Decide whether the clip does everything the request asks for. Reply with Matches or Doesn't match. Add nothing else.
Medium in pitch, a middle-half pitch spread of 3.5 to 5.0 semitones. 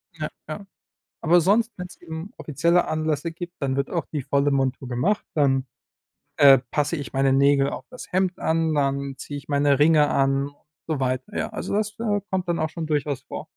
Matches